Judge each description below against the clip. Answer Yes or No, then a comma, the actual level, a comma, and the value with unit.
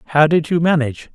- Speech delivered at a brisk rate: Yes, fast, 210 wpm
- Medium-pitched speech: Yes, medium, 155 Hz